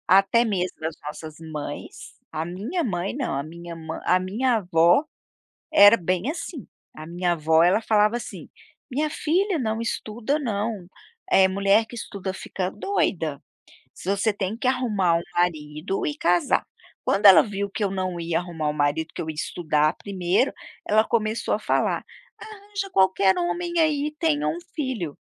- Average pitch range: No, wide, 5.9 semitones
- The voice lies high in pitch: Yes, high, 195 Hz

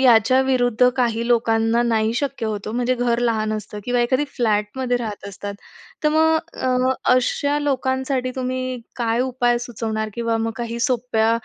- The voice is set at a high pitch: Yes, high, 240 Hz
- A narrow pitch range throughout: Yes, narrow, 2.3 semitones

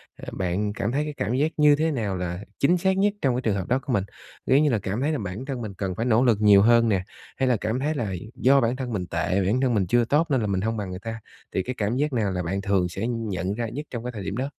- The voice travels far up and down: No, average, 5.0 semitones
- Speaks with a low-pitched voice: Yes, low, 115 Hz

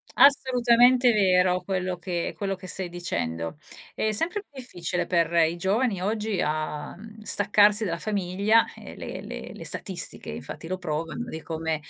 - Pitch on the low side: No, medium, 185 Hz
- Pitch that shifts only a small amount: No, average, 4.3 semitones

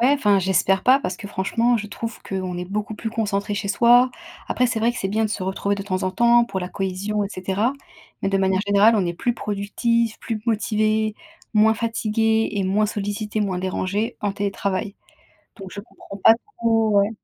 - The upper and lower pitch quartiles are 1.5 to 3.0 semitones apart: Yes, narrow, 2.4 semitones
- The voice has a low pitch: No, high, 210 Hz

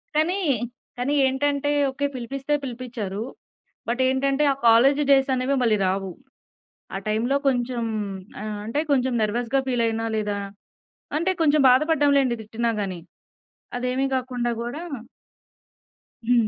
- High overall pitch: Yes, very high, 250 Hz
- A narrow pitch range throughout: No, average, 3.1 semitones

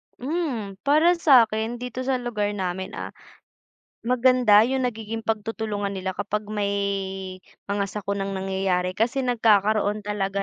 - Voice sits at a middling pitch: No, high, 215 Hz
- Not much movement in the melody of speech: No, average, 3.6 semitones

